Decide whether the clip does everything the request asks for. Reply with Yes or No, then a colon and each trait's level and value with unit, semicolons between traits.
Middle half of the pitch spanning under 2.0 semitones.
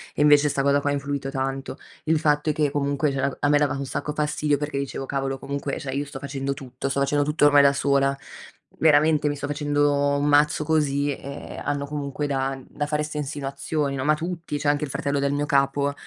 Yes: narrow, 1.2 semitones